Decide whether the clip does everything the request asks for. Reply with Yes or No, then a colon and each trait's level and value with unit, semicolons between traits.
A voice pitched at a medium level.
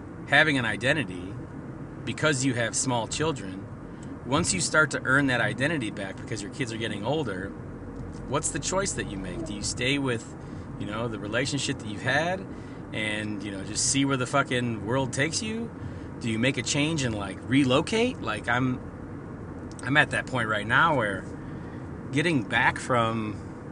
No: low, 125 Hz